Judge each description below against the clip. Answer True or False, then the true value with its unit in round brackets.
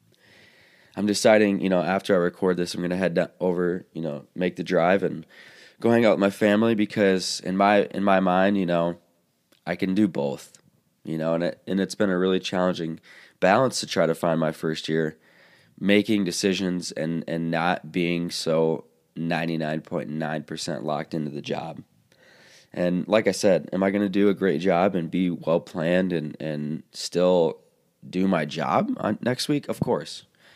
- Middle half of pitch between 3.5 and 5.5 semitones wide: False (2.8 semitones)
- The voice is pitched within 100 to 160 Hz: False (90 Hz)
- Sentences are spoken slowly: False (190 wpm)